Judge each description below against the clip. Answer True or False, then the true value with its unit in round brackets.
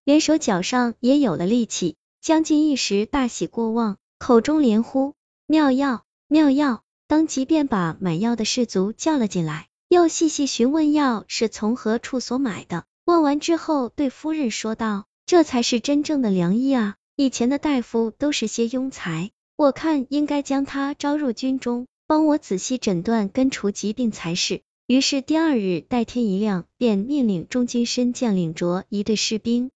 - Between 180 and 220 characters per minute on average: False (250 characters per minute)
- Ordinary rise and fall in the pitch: True (4.7 semitones)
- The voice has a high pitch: True (245 Hz)